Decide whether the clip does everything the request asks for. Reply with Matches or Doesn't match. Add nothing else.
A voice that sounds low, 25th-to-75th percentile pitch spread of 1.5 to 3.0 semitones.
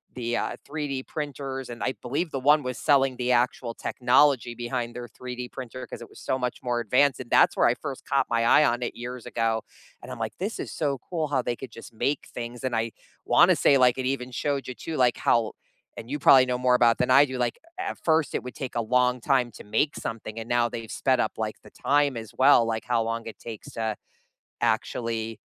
Matches